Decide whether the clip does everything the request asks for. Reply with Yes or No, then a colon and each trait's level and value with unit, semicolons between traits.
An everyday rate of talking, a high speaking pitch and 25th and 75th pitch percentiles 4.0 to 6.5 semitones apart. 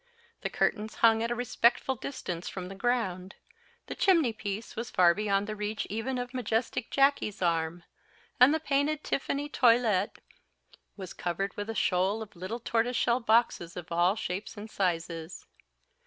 Yes: average, 165 wpm; high, 215 Hz; average, 4.7 semitones